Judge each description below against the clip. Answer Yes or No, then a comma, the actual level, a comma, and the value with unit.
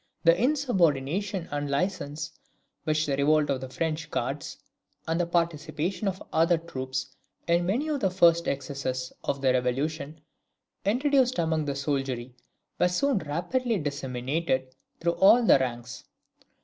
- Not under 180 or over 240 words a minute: No, slow, 135 wpm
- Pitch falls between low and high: Yes, medium, 155 Hz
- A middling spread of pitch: Yes, average, 4.6 semitones